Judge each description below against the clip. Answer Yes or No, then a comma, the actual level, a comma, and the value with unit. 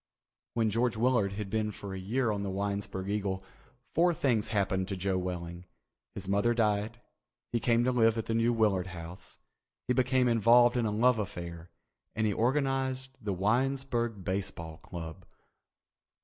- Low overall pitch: Yes, low, 105 Hz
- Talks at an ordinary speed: Yes, average, 165 wpm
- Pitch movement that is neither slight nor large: Yes, average, 4.0 semitones